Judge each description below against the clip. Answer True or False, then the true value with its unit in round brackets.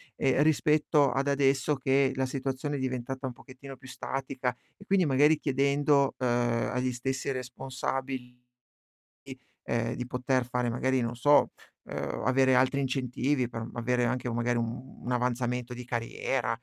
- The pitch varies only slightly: True (1.7 semitones)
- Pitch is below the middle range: True (130 Hz)